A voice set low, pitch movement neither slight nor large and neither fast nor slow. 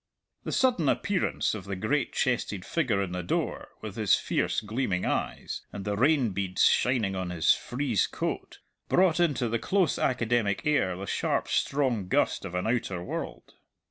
No: low, 115 Hz; wide, 6.4 semitones; average, 170 wpm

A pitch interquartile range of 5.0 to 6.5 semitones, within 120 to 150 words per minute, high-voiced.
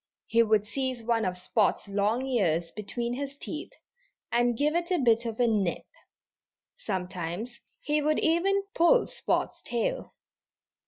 Yes: wide, 5.5 semitones; average, 145 wpm; high, 235 Hz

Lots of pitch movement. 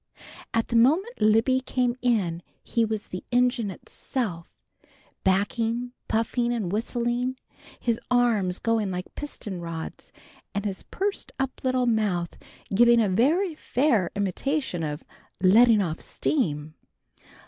No: average, 4.6 semitones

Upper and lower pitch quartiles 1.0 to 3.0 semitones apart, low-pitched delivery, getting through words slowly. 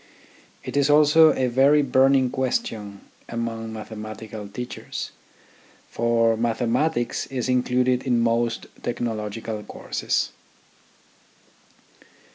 Yes: narrow, 2.6 semitones; low, 120 Hz; slow, 85 wpm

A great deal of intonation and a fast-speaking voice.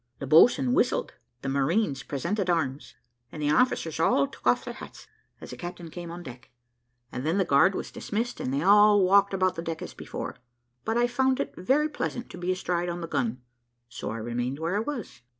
Yes: wide, 6.5 semitones; fast, 215 wpm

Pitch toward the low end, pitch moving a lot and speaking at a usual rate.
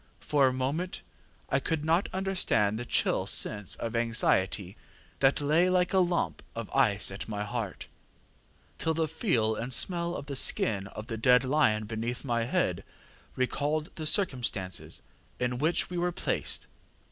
Yes: low, 130 Hz; wide, 6.3 semitones; average, 160 wpm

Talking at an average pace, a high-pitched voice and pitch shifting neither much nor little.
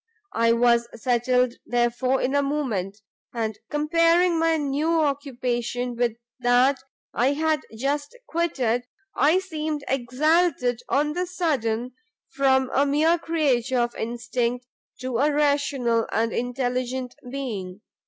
No: slow, 120 wpm; very high, 260 Hz; average, 3.8 semitones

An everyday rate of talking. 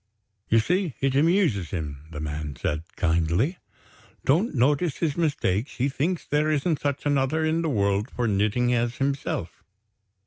Yes: average, 150 wpm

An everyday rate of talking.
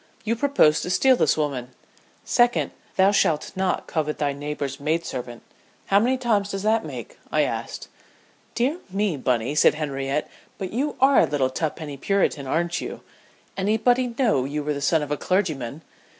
Yes: average, 170 wpm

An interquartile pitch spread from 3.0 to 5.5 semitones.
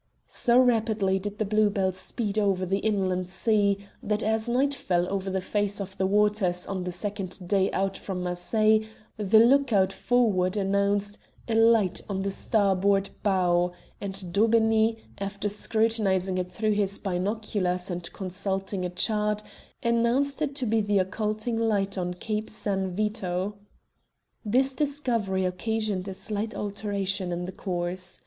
No: narrow, 2.5 semitones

